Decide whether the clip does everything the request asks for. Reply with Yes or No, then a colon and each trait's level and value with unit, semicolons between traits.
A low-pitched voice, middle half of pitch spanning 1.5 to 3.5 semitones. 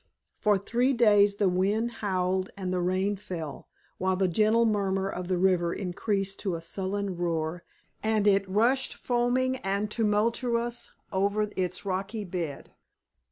No: high, 195 Hz; average, 2.8 semitones